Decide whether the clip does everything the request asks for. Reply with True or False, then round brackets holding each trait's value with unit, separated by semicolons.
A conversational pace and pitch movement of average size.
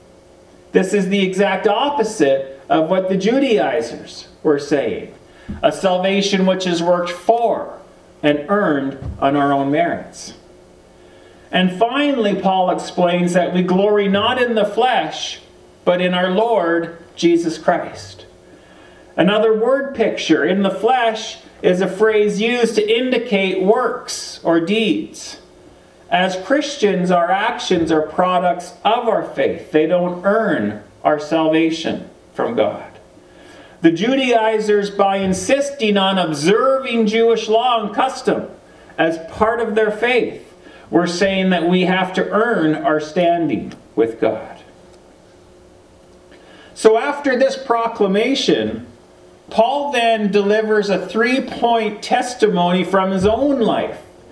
False (125 wpm; 4.6 semitones)